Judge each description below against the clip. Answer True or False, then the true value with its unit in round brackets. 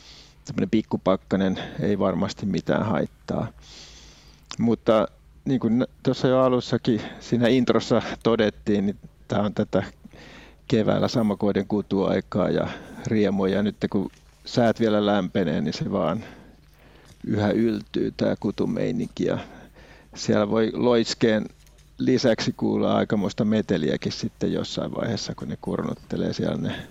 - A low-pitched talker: True (105 Hz)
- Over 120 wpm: False (115 wpm)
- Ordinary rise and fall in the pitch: False (2.3 semitones)